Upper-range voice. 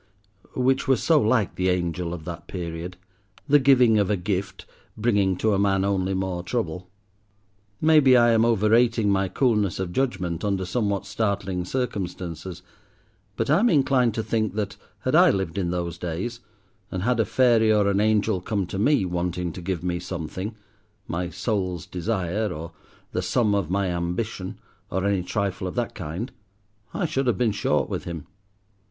No: low, 100 Hz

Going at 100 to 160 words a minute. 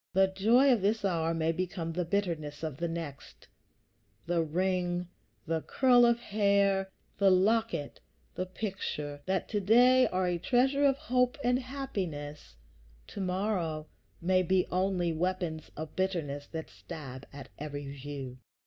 Yes: average, 145 wpm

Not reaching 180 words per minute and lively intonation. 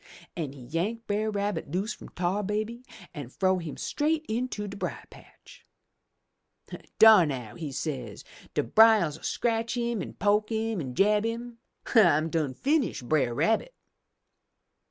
Yes: average, 145 wpm; wide, 6.4 semitones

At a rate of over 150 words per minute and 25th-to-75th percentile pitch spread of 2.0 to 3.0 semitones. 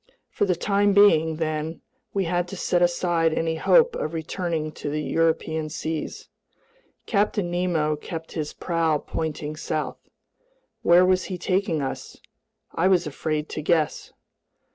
No: average, 140 wpm; narrow, 2.6 semitones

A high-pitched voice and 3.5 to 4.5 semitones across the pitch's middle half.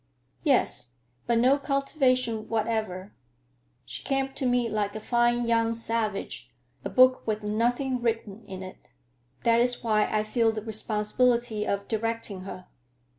No: high, 230 Hz; narrow, 2.4 semitones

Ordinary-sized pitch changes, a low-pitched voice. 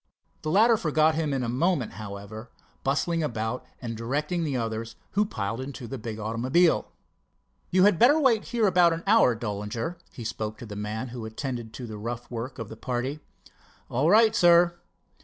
No: wide, 7.2 semitones; low, 130 Hz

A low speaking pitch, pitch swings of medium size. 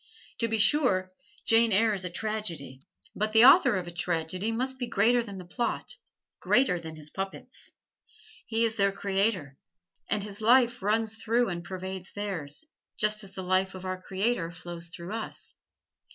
No: high, 200 Hz; average, 3.8 semitones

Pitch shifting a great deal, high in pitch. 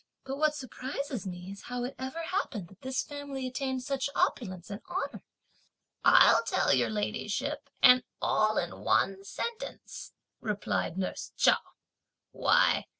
Yes: wide, 6.1 semitones; very high, 255 Hz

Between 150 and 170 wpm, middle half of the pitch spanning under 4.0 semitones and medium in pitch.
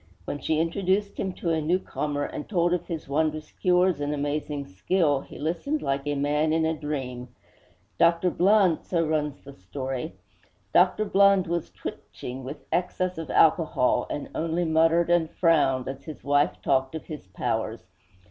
Yes: average, 165 wpm; average, 3.3 semitones; medium, 155 Hz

